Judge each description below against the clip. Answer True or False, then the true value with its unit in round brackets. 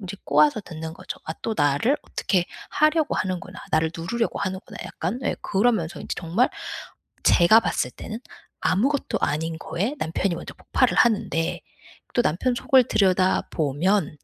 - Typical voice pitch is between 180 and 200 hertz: True (185 Hz)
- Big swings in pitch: True (5.7 semitones)